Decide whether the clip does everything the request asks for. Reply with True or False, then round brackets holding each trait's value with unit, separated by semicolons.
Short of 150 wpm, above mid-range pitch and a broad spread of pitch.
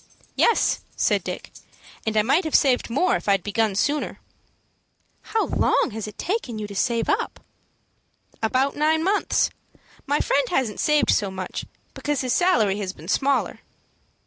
False (160 wpm; 250 Hz; 6.0 semitones)